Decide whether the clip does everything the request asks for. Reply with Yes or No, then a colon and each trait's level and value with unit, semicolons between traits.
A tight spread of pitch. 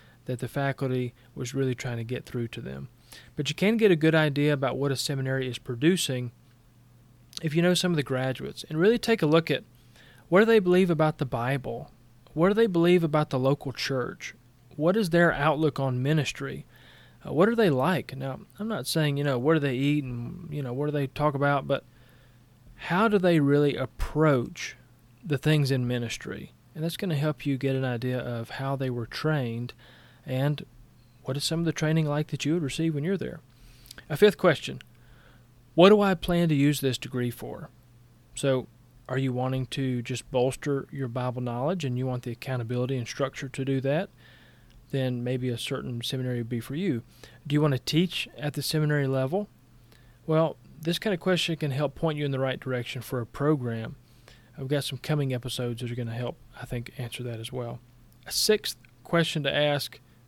No: average, 3.9 semitones